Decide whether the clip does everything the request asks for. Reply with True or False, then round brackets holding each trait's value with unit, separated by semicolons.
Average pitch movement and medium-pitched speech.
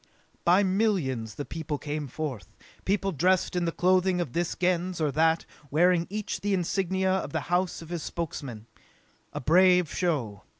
True (3.4 semitones; 175 Hz)